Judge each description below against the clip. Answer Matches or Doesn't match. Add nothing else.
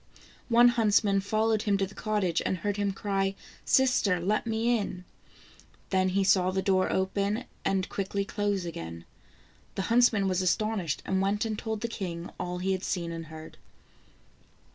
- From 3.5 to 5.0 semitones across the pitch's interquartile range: Doesn't match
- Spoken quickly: Doesn't match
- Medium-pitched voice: Doesn't match